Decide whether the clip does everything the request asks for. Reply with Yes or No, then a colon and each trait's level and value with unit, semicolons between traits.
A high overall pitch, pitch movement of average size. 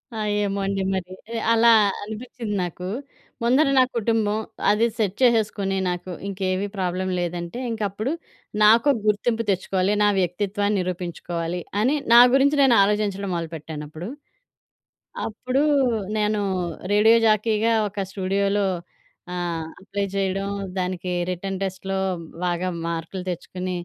Yes: high, 195 Hz; average, 3.0 semitones